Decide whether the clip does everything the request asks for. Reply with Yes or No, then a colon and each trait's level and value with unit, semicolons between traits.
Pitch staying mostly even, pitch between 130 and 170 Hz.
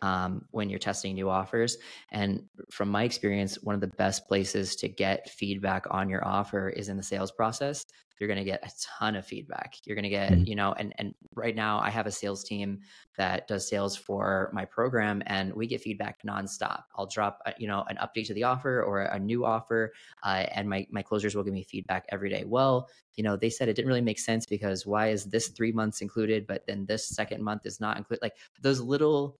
No: narrow, 2.3 semitones; low, 105 Hz